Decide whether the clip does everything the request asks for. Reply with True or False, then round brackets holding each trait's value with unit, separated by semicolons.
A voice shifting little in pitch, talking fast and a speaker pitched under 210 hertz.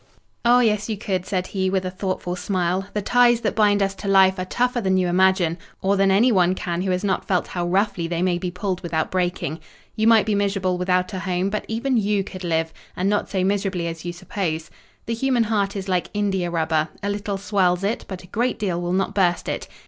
True (2.3 semitones; 230 wpm; 190 Hz)